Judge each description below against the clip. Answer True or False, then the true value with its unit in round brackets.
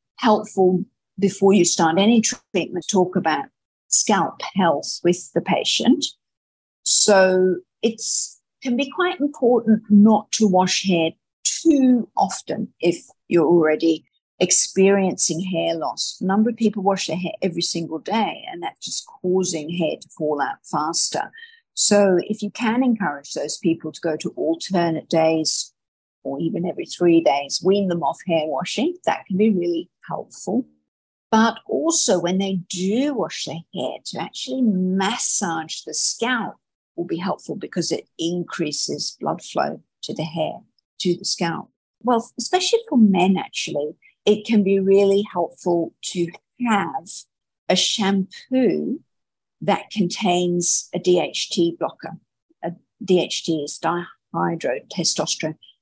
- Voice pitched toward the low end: False (185 Hz)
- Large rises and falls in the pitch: False (4.3 semitones)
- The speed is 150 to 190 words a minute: False (135 wpm)